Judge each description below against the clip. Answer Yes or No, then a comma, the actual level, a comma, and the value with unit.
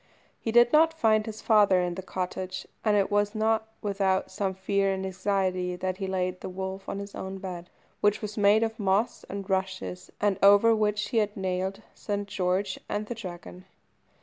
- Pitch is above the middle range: Yes, high, 195 Hz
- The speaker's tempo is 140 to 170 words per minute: No, average, 190 wpm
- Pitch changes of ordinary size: No, narrow, 1.9 semitones